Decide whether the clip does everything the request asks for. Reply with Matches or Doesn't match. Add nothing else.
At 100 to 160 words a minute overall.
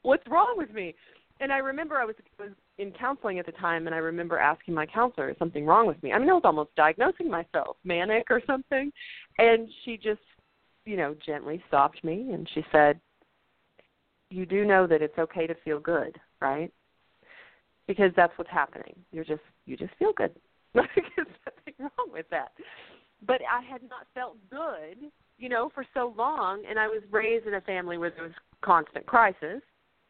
Doesn't match